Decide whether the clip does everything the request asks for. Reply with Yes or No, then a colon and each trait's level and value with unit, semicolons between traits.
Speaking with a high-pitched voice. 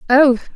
Yes: very high, 265 Hz